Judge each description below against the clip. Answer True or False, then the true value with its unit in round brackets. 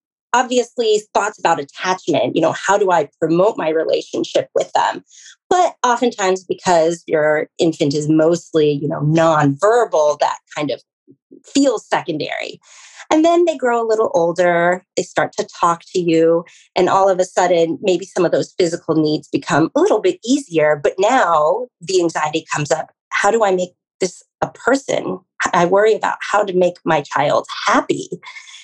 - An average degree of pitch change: False (6.5 semitones)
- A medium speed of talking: True (170 wpm)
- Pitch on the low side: False (185 Hz)